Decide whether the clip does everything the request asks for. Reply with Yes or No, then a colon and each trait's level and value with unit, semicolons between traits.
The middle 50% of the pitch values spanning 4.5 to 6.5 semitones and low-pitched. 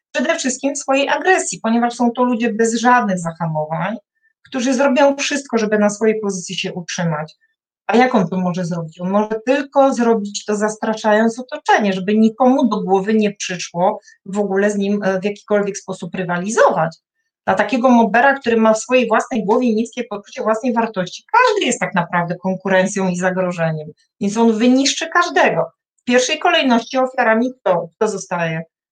No: average, 5.2 semitones; high, 220 Hz